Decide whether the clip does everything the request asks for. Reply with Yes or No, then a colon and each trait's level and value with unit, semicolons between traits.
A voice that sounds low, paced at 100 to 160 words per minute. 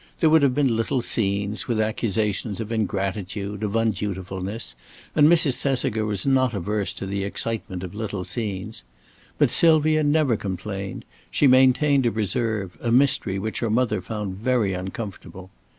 Yes: low, 110 Hz; average, 150 wpm